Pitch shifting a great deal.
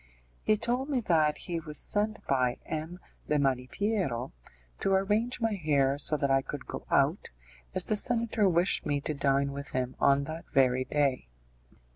Yes: wide, 6.9 semitones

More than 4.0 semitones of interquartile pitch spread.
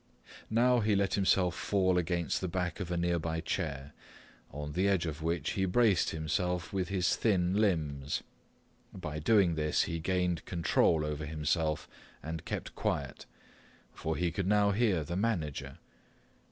No: average, 3.6 semitones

